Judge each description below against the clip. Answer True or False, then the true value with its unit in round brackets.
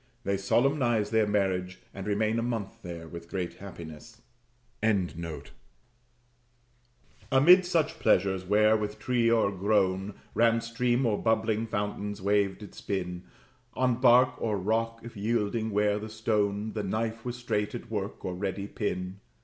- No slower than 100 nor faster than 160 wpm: True (140 wpm)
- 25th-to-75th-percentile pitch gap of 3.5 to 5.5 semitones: False (3.0 semitones)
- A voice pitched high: False (110 Hz)